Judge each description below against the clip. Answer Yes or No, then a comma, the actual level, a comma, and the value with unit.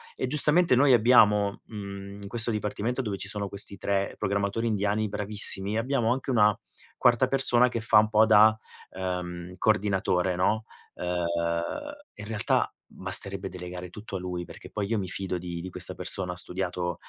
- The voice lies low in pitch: Yes, low, 100 Hz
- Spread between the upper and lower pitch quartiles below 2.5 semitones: No, average, 2.9 semitones